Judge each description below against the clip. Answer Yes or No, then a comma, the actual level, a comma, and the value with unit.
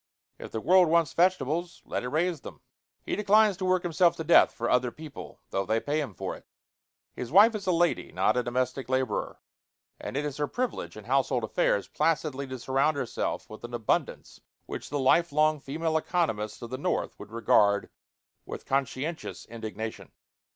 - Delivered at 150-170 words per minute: No, average, 180 wpm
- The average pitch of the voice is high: No, medium, 140 Hz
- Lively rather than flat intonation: Yes, wide, 5.8 semitones